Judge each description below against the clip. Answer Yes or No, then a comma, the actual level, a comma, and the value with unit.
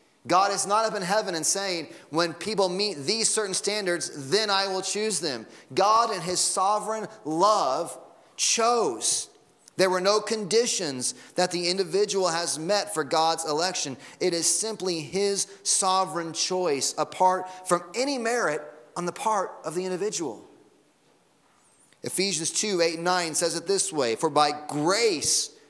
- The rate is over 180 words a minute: No, average, 150 wpm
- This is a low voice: No, medium, 185 Hz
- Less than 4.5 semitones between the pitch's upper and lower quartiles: Yes, average, 3.6 semitones